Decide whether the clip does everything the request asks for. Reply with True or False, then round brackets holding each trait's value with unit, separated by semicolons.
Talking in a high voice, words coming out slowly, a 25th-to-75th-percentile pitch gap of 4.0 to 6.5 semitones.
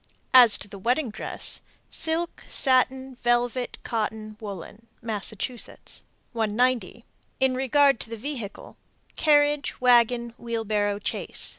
False (240 Hz; 110 wpm; 3.0 semitones)